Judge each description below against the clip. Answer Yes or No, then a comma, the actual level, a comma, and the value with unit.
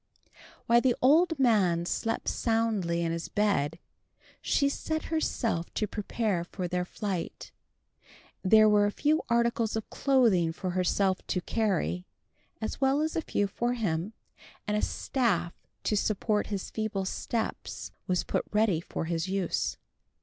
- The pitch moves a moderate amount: Yes, average, 4.6 semitones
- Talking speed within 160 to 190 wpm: No, average, 145 wpm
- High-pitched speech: Yes, high, 210 Hz